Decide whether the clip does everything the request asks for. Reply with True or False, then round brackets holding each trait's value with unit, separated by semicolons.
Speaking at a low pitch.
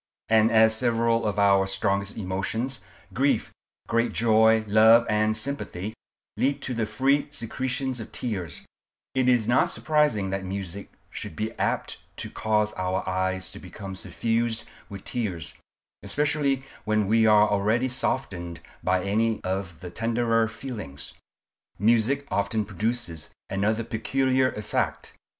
True (110 Hz)